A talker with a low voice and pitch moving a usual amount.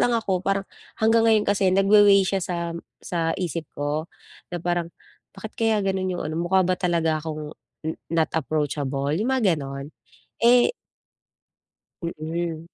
No: medium, 175 Hz; average, 3.7 semitones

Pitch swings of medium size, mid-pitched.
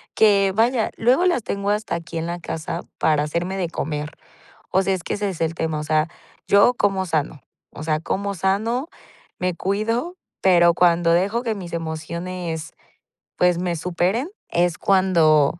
Yes: average, 3.4 semitones; medium, 180 Hz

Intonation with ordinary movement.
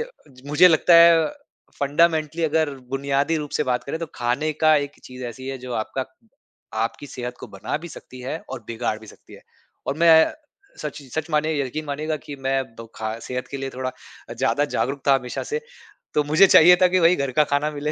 Yes: average, 3.4 semitones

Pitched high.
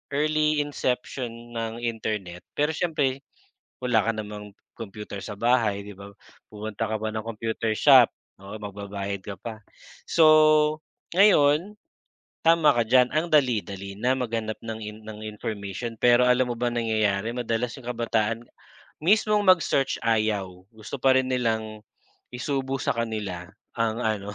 No: low, 115 Hz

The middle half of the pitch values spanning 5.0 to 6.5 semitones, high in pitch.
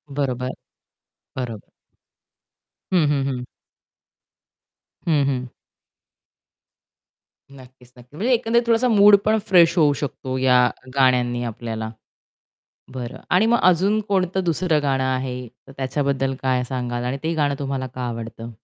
No: wide, 5.4 semitones; low, 135 Hz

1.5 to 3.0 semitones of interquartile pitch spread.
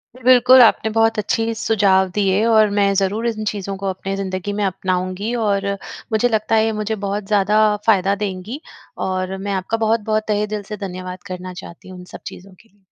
Yes: narrow, 2.6 semitones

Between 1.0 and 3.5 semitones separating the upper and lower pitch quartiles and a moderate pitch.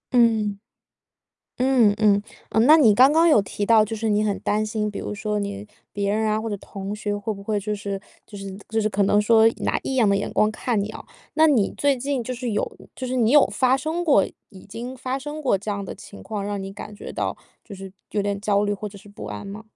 No: average, 3.0 semitones; high, 215 Hz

